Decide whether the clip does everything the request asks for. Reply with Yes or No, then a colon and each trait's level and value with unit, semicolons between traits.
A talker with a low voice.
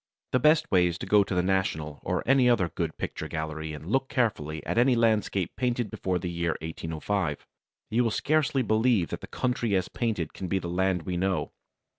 Yes: very low, 95 Hz